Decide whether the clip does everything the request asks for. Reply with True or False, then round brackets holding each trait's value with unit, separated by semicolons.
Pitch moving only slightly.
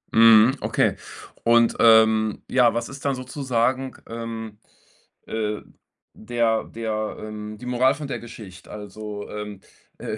True (2.2 semitones)